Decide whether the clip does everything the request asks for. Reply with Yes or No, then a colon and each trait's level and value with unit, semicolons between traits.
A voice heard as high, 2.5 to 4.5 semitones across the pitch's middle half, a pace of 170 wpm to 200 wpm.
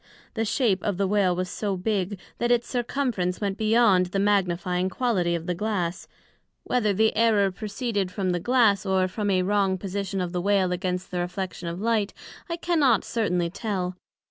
Yes: high, 195 Hz; average, 3.2 semitones; average, 180 wpm